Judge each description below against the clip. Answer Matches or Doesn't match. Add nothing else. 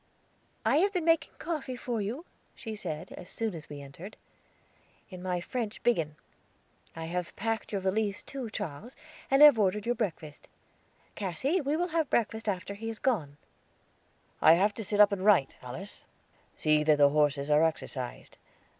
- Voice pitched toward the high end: Matches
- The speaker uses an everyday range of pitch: Doesn't match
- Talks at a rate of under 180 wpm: Matches